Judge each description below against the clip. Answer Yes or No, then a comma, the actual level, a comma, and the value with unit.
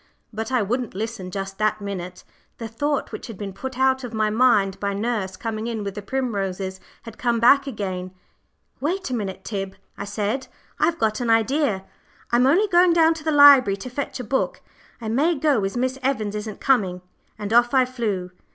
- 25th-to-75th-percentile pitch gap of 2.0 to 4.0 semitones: No, average, 4.7 semitones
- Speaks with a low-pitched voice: No, high, 225 Hz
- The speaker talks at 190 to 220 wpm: Yes, average, 195 wpm